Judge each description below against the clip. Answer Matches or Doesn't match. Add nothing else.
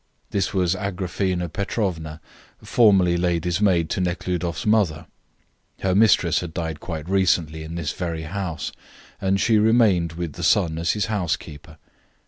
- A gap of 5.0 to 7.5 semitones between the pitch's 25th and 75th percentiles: Doesn't match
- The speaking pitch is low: Matches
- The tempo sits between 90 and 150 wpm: Matches